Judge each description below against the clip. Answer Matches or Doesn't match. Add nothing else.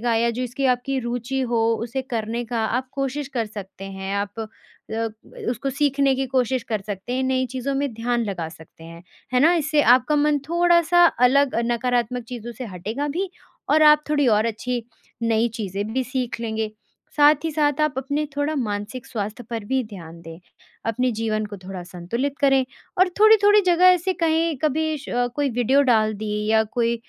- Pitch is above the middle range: Matches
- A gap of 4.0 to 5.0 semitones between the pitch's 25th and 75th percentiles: Matches